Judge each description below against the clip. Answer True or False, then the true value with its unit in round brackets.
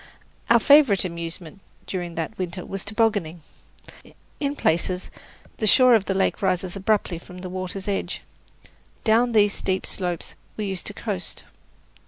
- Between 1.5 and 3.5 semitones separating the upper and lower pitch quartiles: True (3.2 semitones)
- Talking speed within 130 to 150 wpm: True (145 wpm)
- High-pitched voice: True (195 Hz)